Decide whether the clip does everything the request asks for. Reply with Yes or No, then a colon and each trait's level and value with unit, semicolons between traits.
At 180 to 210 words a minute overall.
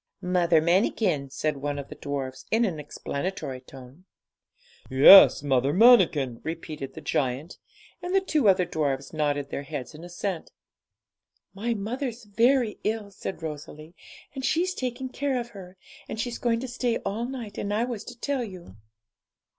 No: average, 160 wpm